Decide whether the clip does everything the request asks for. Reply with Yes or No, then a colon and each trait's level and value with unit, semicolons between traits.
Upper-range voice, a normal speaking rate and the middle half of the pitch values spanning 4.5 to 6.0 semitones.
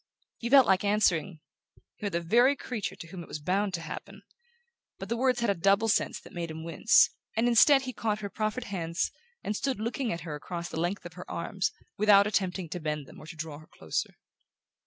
No: high, 195 Hz; fast, 220 wpm; average, 4.8 semitones